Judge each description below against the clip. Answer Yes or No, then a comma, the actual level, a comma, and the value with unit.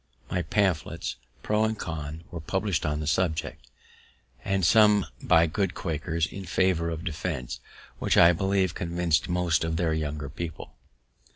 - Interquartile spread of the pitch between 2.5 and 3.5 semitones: Yes, average, 3.0 semitones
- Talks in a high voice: No, very low, 85 Hz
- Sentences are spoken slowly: No, average, 150 wpm